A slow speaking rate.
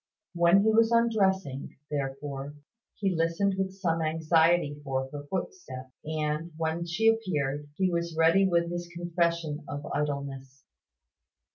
Yes: slow, 130 wpm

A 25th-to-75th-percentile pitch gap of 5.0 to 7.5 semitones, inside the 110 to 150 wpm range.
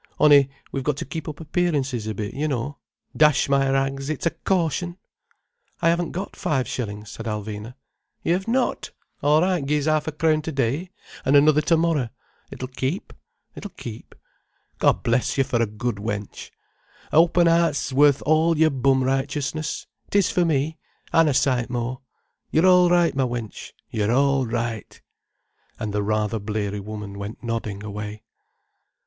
No: wide, 5.4 semitones; average, 165 wpm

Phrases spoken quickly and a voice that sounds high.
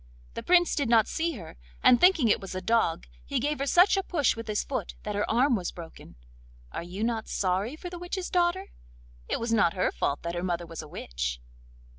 Yes: fast, 225 wpm; high, 230 Hz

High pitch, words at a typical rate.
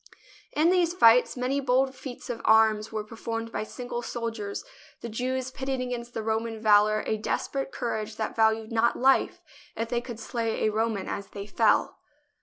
Yes: high, 230 Hz; average, 180 wpm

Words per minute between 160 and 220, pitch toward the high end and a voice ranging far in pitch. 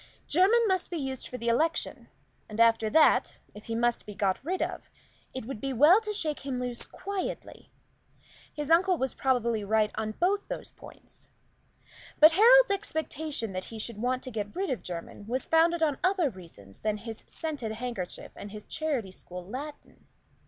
Yes: average, 180 wpm; very high, 255 Hz; wide, 6.9 semitones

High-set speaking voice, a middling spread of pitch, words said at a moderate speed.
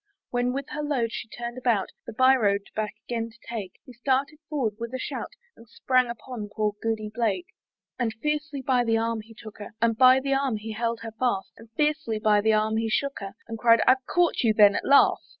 No: high, 230 Hz; average, 3.0 semitones; fast, 225 wpm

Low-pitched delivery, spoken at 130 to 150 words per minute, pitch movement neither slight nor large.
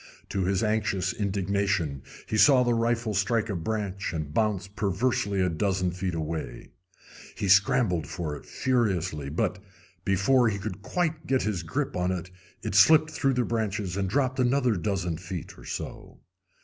No: low, 100 Hz; average, 160 wpm; average, 4.3 semitones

